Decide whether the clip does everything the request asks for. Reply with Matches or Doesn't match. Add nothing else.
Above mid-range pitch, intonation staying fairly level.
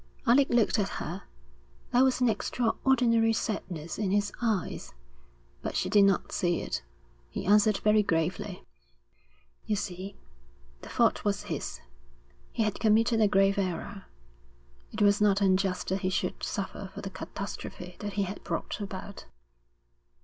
Matches